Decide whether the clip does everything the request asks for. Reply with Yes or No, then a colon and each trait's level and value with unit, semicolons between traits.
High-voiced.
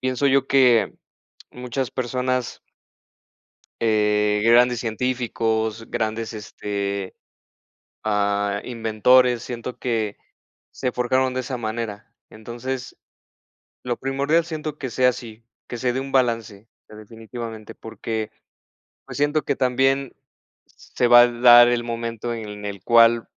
No: low, 120 Hz